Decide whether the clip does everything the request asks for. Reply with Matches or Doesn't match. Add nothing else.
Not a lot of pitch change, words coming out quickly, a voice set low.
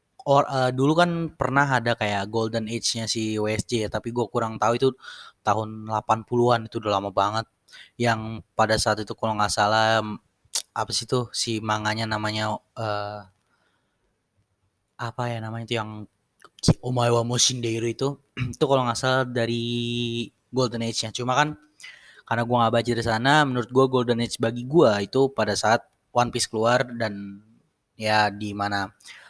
Matches